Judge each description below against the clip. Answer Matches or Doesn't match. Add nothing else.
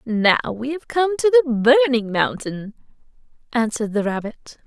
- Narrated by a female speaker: Matches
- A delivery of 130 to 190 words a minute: Matches